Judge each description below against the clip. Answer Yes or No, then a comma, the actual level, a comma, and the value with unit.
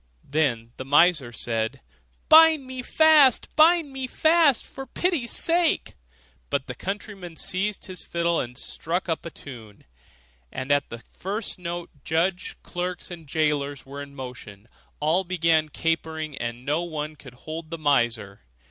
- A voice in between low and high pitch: Yes, medium, 165 Hz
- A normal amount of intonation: No, wide, 5.8 semitones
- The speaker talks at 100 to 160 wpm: Yes, average, 150 wpm